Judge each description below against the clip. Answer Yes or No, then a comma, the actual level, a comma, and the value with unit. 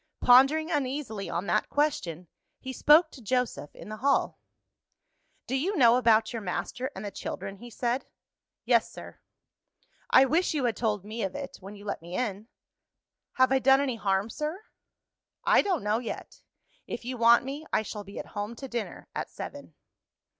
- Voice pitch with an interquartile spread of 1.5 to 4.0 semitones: No, average, 4.6 semitones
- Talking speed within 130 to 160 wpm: No, average, 180 wpm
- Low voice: No, high, 240 Hz